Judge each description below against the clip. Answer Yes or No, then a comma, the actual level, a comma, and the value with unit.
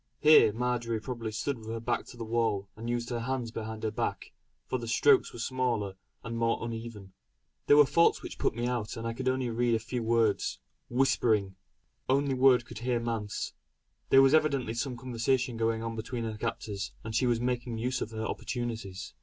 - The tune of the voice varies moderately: No, narrow, 2.0 semitones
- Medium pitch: No, low, 115 Hz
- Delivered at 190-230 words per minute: Yes, average, 200 wpm